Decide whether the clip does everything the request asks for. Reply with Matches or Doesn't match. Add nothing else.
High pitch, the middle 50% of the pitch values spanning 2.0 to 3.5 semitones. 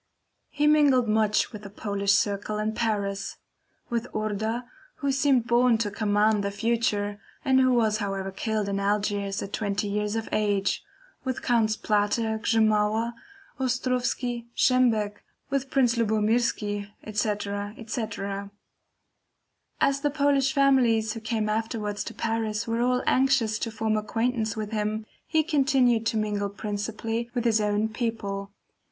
Matches